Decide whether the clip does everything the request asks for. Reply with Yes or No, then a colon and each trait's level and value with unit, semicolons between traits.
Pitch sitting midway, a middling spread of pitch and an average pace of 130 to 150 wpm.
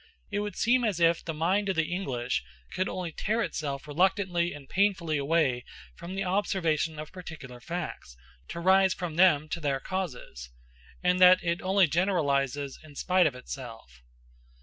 No: medium, 170 Hz; average, 4.7 semitones; average, 165 wpm